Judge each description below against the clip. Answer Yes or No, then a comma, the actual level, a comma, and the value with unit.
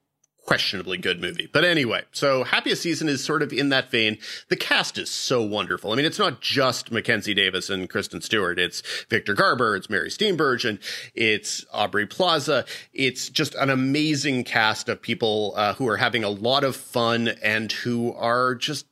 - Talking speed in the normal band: Yes, average, 185 wpm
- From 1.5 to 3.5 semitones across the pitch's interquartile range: No, average, 3.9 semitones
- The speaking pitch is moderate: No, low, 125 Hz